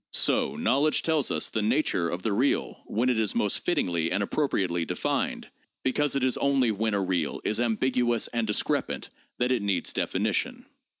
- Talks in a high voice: No, low, 115 Hz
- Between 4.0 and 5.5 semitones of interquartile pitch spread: Yes, average, 4.7 semitones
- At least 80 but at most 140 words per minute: No, average, 175 wpm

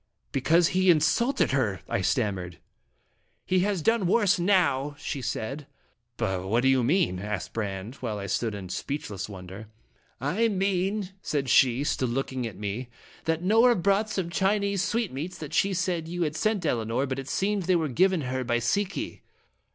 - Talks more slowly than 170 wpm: No, average, 175 wpm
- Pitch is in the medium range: Yes, medium, 145 Hz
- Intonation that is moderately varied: No, wide, 8.2 semitones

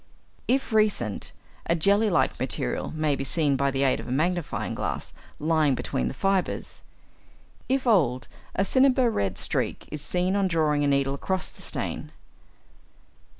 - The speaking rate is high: No, average, 155 wpm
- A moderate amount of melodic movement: No, wide, 6.1 semitones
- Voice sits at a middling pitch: Yes, medium, 160 Hz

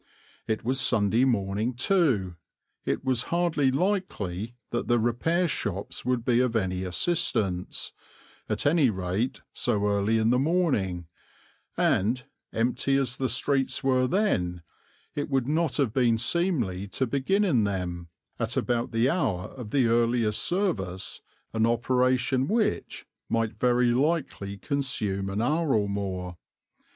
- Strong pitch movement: No, average, 5.0 semitones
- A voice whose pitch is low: Yes, low, 120 Hz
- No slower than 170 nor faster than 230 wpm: No, average, 140 wpm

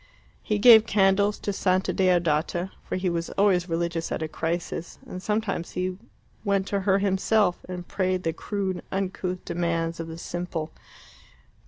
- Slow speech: No, average, 155 wpm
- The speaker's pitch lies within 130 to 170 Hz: No, medium, 185 Hz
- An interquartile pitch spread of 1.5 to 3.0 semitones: Yes, narrow, 2.5 semitones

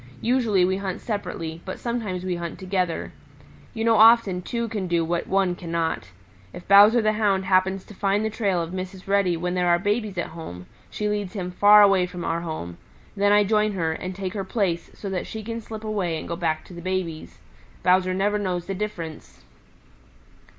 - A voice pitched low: No, high, 190 Hz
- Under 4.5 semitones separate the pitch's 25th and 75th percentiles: Yes, average, 3.0 semitones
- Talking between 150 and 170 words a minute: No, average, 200 wpm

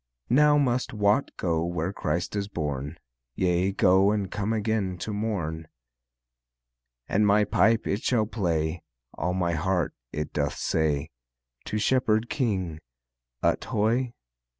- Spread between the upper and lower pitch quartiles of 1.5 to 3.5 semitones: No, average, 4.6 semitones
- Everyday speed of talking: No, slow, 130 wpm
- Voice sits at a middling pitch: No, low, 100 Hz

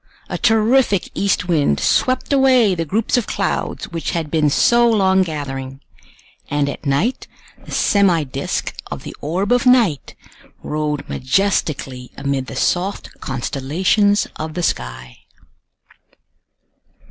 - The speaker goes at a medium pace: No, slow, 125 wpm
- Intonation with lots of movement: Yes, wide, 6.6 semitones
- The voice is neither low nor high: Yes, medium, 165 Hz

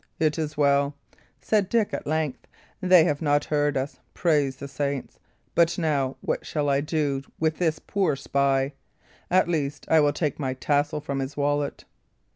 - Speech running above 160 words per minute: Yes, average, 170 wpm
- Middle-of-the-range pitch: Yes, medium, 145 Hz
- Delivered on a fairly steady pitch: Yes, narrow, 2.2 semitones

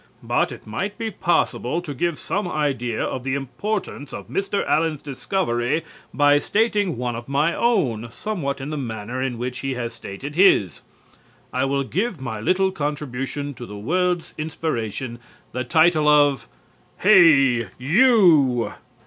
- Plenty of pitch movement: Yes, wide, 5.8 semitones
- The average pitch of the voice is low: No, medium, 145 Hz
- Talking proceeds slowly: No, average, 150 wpm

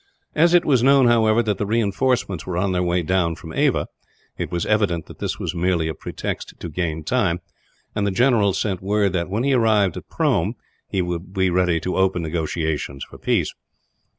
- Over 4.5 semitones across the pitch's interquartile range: No, average, 4.0 semitones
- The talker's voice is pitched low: Yes, very low, 95 Hz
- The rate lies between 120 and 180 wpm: No, average, 195 wpm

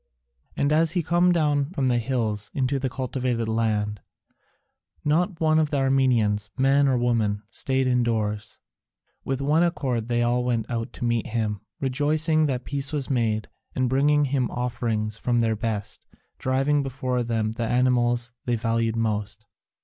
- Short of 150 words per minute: No, average, 155 wpm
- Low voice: Yes, low, 125 Hz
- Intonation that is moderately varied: Yes, average, 3.4 semitones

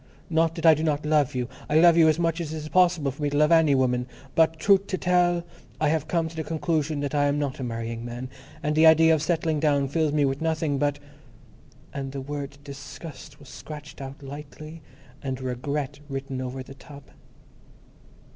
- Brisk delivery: Yes, fast, 210 wpm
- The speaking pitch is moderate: Yes, medium, 150 Hz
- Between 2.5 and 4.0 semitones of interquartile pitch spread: Yes, average, 2.8 semitones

